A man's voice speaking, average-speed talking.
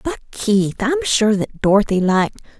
No: female; average, 160 wpm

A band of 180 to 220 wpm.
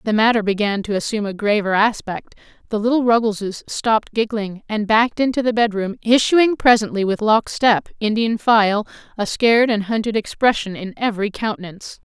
No: average, 170 wpm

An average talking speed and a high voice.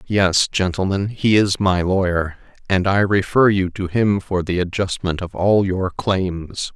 No: average, 170 wpm; very low, 95 Hz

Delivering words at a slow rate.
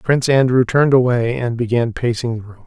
No: fast, 205 wpm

